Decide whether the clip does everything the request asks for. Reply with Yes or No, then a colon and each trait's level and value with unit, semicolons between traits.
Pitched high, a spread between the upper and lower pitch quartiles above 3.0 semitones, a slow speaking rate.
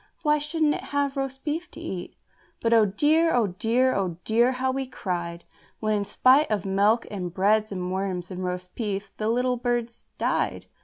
No: high, 225 Hz; wide, 5.4 semitones; average, 190 wpm